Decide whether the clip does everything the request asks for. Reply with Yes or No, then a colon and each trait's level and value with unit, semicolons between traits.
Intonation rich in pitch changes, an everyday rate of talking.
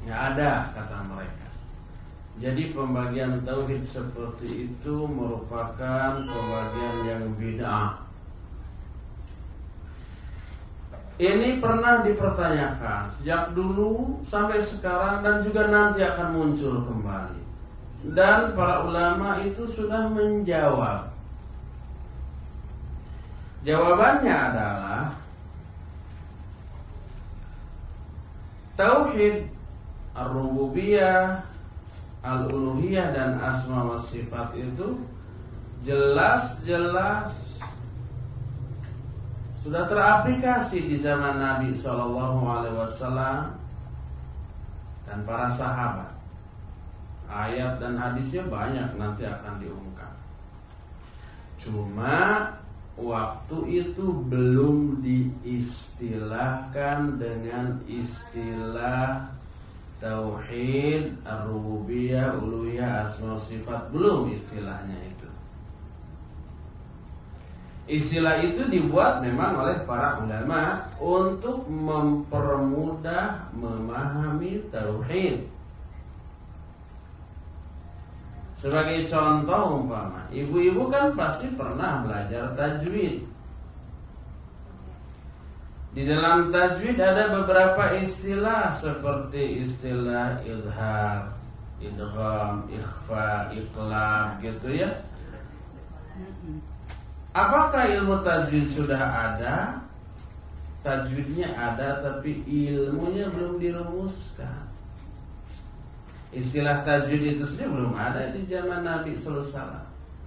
No: wide, 7.6 semitones; slow, 70 wpm